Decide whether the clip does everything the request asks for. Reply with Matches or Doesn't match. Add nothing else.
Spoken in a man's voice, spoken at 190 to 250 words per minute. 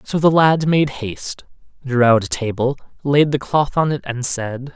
Matches